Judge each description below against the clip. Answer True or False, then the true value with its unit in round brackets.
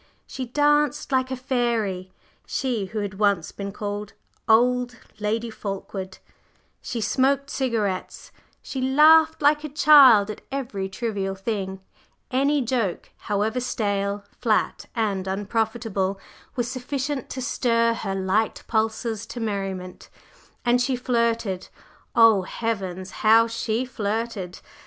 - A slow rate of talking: True (120 wpm)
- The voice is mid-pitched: False (225 Hz)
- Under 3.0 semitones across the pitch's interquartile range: False (4.0 semitones)